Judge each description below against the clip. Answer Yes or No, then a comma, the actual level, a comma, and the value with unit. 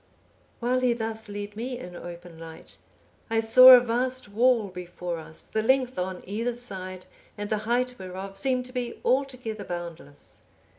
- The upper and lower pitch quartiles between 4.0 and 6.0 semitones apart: Yes, average, 5.3 semitones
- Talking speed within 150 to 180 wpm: Yes, average, 160 wpm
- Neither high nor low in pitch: No, high, 220 Hz